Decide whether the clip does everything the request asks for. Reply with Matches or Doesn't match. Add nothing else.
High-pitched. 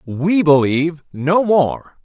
Doesn't match